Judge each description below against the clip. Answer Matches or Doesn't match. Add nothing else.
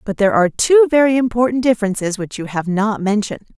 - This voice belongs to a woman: Matches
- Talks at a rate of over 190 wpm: Matches